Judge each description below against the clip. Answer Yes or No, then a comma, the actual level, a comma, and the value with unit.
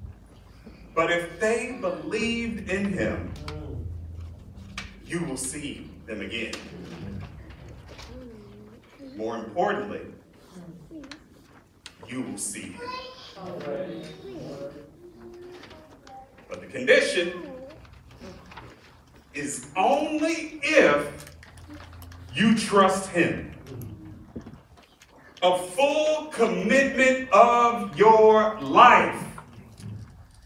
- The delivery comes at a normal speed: No, slow, 65 wpm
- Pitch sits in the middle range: Yes, medium, 170 Hz